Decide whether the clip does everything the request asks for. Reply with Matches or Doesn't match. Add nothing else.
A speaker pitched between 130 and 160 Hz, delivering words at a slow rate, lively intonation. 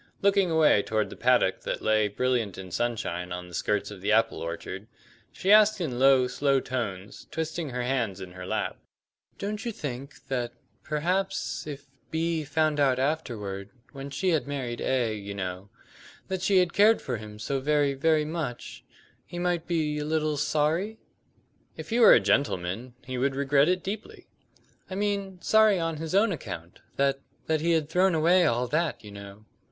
Doesn't match